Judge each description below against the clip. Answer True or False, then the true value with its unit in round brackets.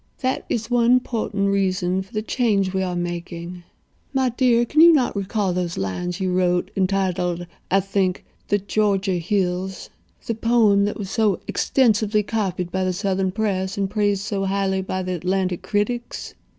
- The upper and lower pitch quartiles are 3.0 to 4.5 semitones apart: False (2.6 semitones)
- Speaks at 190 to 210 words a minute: False (160 wpm)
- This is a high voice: True (195 Hz)